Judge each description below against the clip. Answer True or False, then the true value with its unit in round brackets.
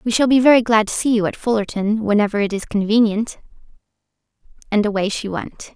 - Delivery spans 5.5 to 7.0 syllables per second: True (6.0 syllables/s)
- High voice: True (215 Hz)